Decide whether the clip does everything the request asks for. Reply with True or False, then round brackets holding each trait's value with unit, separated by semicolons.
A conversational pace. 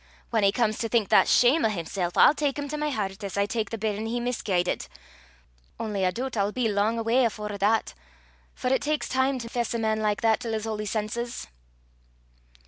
False (215 wpm)